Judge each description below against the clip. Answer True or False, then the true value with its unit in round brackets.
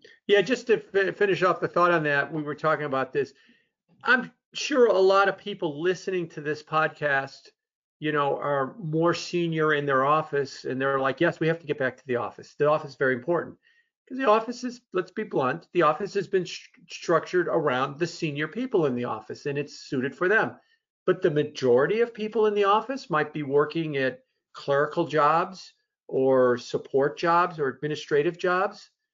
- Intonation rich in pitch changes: True (5.8 semitones)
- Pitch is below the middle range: False (170 Hz)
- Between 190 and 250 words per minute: True (200 wpm)